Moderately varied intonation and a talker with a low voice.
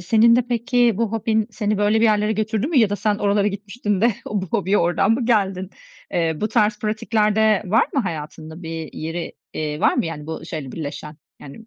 No: average, 4.4 semitones; high, 205 Hz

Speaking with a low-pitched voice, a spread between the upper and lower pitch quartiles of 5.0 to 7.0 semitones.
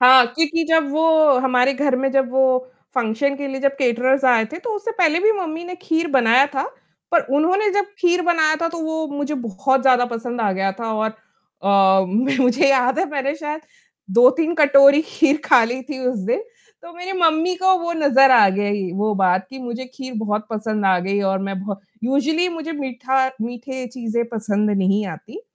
No: very high, 265 Hz; wide, 5.6 semitones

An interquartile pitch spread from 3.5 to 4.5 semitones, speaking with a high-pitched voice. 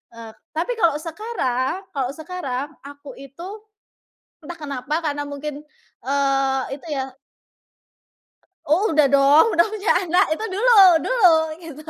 Yes: average, 4.0 semitones; very high, 300 Hz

